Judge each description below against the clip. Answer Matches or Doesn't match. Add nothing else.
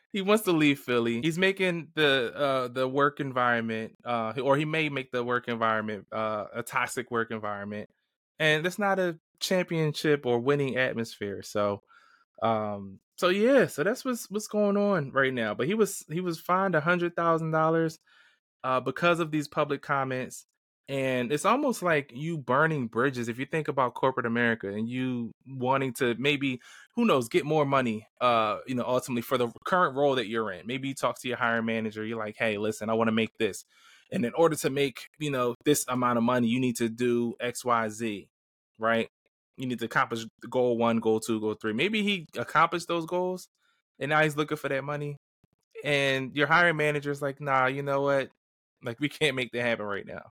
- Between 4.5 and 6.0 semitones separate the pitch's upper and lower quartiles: Matches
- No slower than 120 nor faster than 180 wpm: Doesn't match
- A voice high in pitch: Doesn't match